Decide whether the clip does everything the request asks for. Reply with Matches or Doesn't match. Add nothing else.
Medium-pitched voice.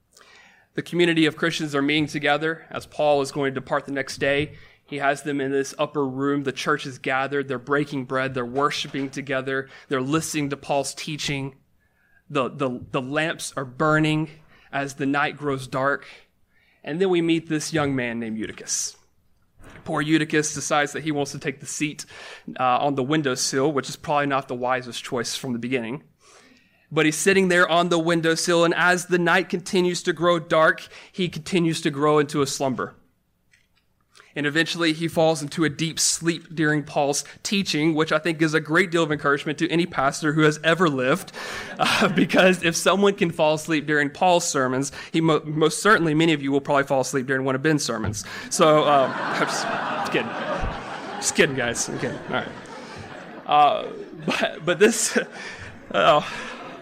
Matches